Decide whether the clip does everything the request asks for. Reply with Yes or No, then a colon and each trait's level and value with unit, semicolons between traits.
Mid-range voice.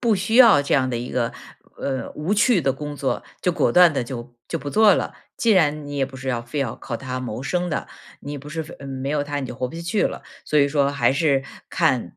Yes: medium, 145 Hz